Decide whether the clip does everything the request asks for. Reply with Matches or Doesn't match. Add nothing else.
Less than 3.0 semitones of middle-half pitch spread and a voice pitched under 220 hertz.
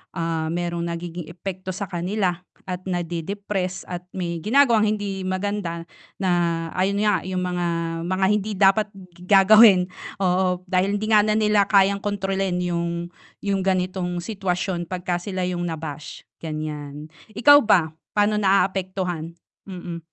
Matches